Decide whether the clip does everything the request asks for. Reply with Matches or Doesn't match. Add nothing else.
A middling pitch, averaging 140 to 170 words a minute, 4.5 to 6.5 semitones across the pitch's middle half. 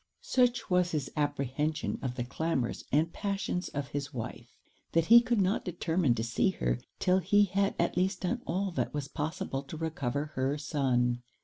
Doesn't match